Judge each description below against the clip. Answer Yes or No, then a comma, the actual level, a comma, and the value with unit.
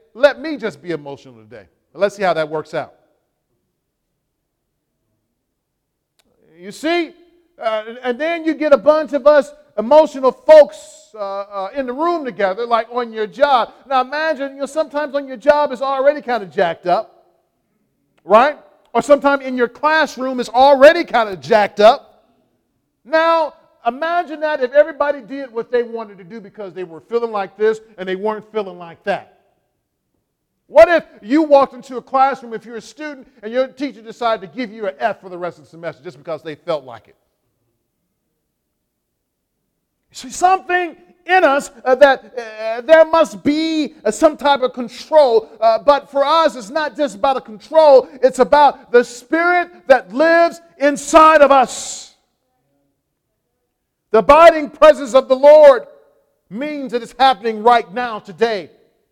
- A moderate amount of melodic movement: No, wide, 5.8 semitones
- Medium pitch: No, very high, 260 Hz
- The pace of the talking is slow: No, average, 165 wpm